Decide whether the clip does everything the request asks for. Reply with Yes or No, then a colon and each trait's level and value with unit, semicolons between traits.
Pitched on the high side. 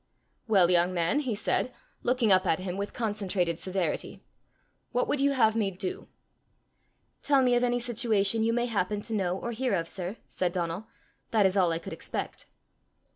Yes: high, 205 Hz